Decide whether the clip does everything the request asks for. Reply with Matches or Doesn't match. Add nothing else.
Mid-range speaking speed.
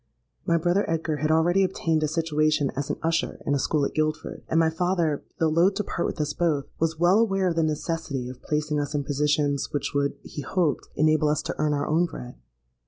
Doesn't match